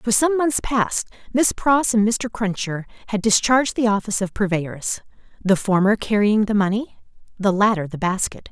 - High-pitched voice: Yes, high, 210 Hz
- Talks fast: No, average, 170 wpm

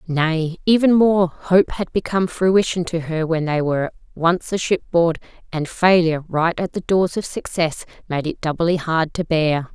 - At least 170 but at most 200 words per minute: Yes, average, 180 wpm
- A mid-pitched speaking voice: Yes, medium, 170 Hz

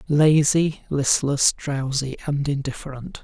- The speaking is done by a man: Yes, male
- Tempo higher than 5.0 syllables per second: No, 3.8 syllables/s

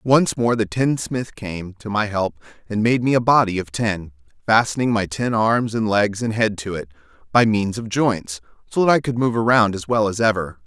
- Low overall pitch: Yes, low, 110 Hz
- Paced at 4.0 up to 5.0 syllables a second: Yes, 4.8 syllables/s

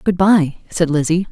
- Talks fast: No, average, 185 wpm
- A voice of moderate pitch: Yes, medium, 175 Hz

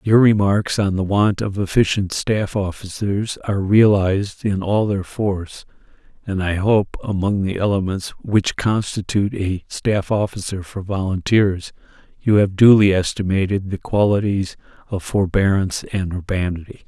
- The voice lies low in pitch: Yes, low, 100 Hz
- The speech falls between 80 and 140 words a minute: Yes, slow, 135 wpm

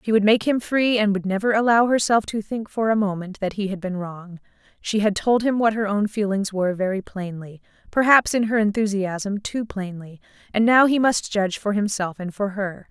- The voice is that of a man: No, female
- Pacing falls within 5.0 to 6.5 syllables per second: Yes, 5.2 syllables/s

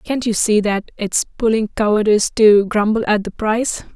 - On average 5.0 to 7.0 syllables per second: Yes, 5.1 syllables/s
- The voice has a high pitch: Yes, high, 215 Hz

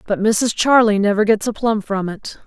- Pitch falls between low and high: No, high, 215 Hz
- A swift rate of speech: Yes, fast, 220 wpm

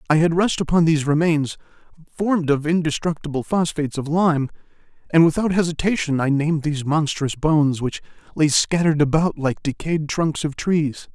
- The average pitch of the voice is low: No, medium, 155 Hz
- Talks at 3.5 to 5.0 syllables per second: No, 5.4 syllables/s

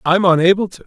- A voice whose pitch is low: No, medium, 180 Hz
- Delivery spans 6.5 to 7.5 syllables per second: Yes, 6.6 syllables/s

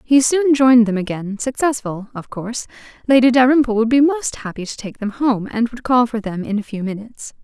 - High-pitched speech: Yes, high, 235 Hz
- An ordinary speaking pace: No, fast, 220 wpm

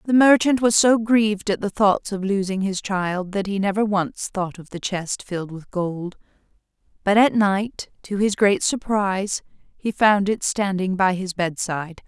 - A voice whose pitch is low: No, high, 200 Hz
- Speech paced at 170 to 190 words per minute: Yes, average, 185 wpm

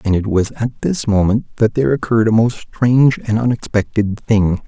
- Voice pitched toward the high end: No, low, 110 Hz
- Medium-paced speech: Yes, average, 190 wpm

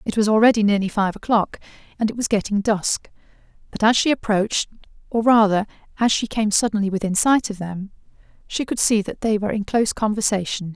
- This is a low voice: No, high, 210 Hz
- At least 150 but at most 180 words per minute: No, average, 190 wpm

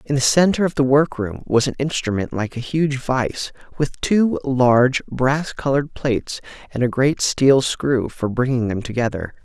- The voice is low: Yes, low, 130 Hz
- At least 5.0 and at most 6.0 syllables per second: No, 4.6 syllables/s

